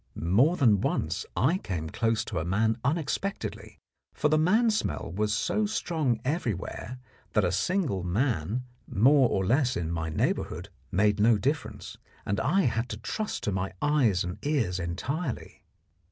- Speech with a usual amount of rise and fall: No, wide, 7.6 semitones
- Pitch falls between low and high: No, low, 115 Hz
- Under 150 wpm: No, average, 155 wpm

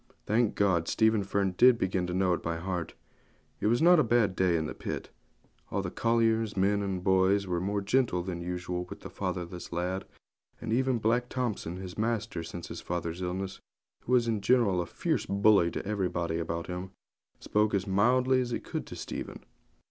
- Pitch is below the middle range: Yes, very low, 95 Hz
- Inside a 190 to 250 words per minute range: Yes, average, 195 wpm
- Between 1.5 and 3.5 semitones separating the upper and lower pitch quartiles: No, average, 4.1 semitones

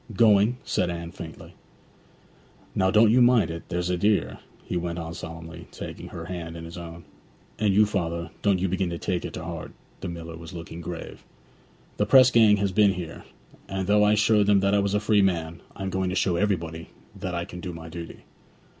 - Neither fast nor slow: No, fast, 215 wpm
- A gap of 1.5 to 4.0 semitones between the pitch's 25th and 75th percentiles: Yes, average, 3.4 semitones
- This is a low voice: Yes, very low, 90 Hz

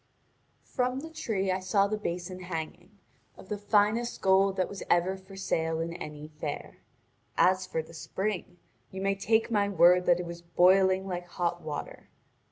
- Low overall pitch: No, medium, 185 Hz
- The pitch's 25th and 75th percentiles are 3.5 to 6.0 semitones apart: No, narrow, 2.4 semitones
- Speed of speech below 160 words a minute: No, average, 175 wpm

